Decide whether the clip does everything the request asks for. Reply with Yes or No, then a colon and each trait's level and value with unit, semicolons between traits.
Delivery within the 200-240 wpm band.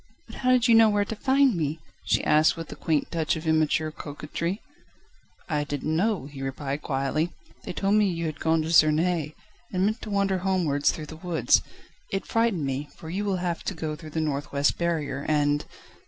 Yes: fast, 205 wpm